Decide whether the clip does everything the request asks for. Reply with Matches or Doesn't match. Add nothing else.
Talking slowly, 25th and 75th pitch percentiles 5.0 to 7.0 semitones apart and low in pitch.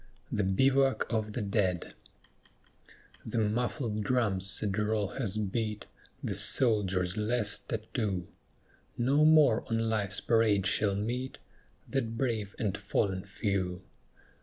Doesn't match